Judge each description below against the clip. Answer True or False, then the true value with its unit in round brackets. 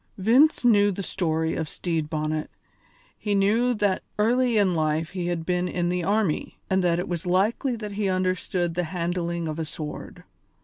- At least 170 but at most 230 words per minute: True (180 wpm)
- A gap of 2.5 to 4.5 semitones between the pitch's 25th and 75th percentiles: True (3.6 semitones)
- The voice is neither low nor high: True (180 Hz)